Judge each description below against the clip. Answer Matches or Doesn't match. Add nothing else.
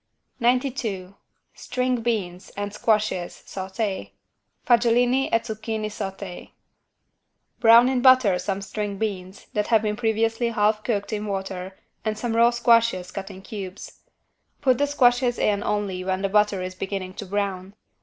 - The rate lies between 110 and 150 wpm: Matches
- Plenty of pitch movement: Doesn't match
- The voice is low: Doesn't match